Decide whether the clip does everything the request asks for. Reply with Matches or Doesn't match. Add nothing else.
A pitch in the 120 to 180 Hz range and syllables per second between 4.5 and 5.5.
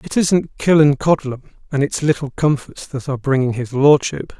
Matches